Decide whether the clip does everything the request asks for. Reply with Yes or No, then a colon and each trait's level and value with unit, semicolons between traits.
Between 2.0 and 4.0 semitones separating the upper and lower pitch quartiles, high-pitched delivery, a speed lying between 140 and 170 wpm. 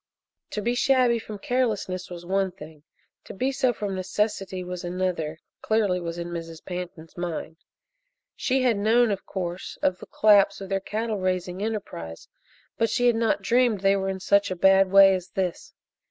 No: average, 3.3 semitones; high, 195 Hz; average, 180 wpm